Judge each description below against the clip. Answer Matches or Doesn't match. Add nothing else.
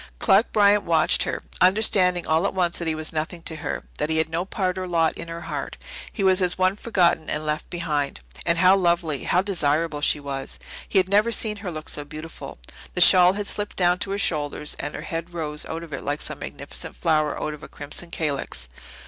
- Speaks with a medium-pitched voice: Matches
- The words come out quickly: Matches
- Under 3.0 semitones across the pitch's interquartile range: Doesn't match